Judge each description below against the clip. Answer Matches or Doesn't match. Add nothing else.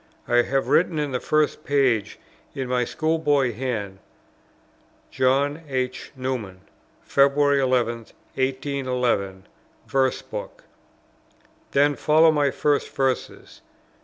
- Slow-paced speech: Matches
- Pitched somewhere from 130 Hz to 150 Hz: Matches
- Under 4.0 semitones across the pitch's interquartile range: Matches